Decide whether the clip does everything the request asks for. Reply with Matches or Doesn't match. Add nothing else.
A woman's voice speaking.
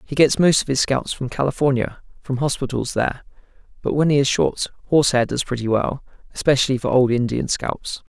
Doesn't match